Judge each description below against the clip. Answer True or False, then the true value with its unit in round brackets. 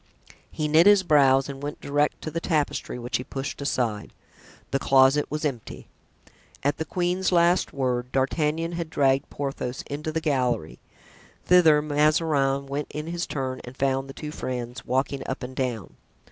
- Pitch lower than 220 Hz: True (140 Hz)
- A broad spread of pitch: False (2.9 semitones)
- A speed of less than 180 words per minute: True (165 wpm)